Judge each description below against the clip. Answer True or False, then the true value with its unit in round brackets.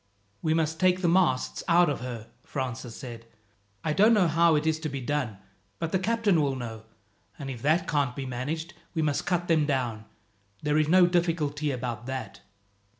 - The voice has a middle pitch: True (150 Hz)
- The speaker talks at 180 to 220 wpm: True (190 wpm)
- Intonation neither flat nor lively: True (4.6 semitones)